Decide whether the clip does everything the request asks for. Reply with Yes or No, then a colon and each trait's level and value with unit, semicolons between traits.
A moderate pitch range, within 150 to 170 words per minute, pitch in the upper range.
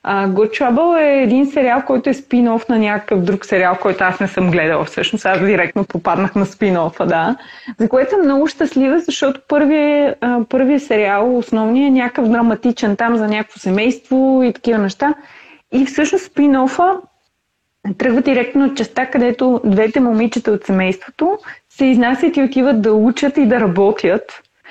Yes: average, 4.7 semitones; fast, 165 wpm; high, 245 Hz